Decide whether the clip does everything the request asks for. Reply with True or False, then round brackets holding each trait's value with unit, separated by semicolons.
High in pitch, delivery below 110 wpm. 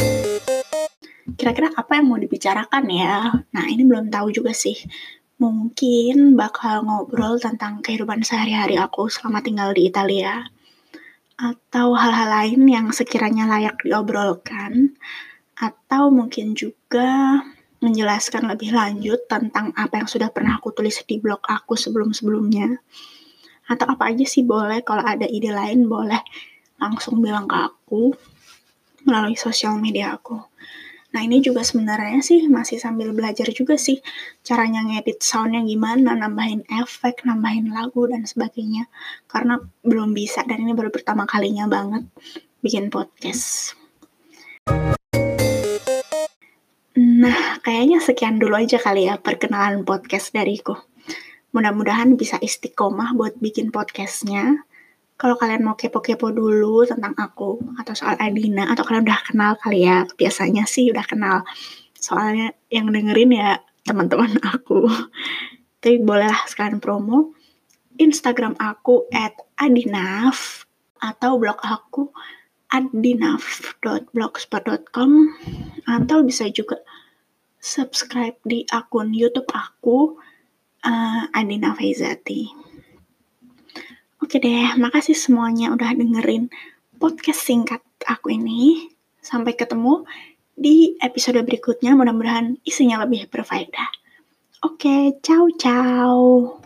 False (235 Hz; 115 wpm)